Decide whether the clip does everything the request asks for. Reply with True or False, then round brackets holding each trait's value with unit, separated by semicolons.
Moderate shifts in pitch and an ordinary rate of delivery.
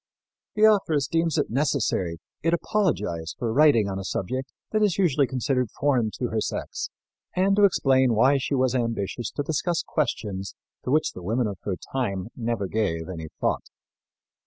False (6.5 semitones; 170 wpm)